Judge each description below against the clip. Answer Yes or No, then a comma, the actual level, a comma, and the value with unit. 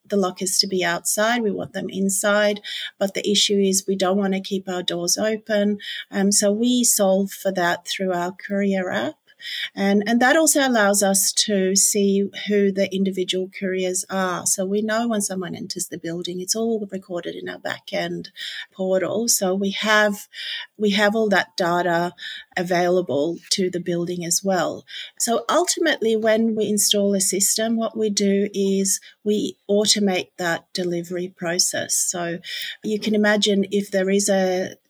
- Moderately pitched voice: No, high, 195 Hz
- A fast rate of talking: No, average, 165 wpm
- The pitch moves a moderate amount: No, narrow, 2.2 semitones